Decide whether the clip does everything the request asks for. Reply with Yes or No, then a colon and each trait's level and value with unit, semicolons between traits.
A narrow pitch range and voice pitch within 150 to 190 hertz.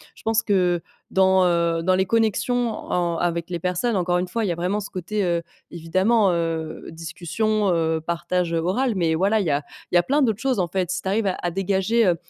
No: average, 3.6 semitones; medium, 185 Hz